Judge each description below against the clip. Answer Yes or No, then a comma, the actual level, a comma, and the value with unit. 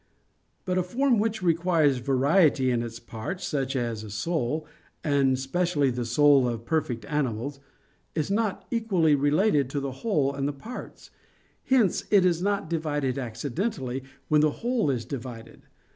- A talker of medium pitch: Yes, medium, 145 Hz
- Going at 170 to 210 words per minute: No, average, 155 wpm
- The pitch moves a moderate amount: No, wide, 5.7 semitones